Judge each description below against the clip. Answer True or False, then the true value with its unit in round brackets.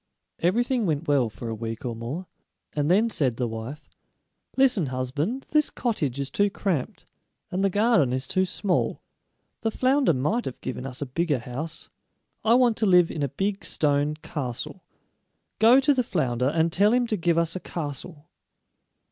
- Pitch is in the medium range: True (165 Hz)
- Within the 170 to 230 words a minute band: True (175 wpm)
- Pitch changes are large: True (7.8 semitones)